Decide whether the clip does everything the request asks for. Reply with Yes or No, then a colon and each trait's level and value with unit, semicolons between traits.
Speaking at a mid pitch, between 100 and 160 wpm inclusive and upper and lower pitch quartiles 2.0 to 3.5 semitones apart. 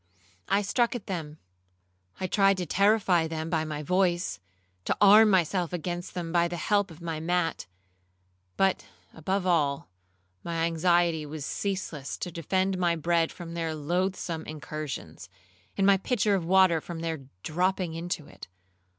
Yes: medium, 170 Hz; average, 150 wpm; average, 2.9 semitones